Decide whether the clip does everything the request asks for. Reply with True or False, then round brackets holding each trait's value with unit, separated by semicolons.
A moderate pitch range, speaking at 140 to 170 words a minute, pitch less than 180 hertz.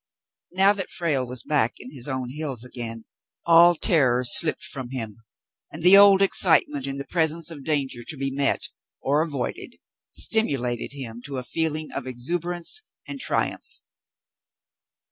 True (4.7 semitones; 150 wpm; 140 Hz)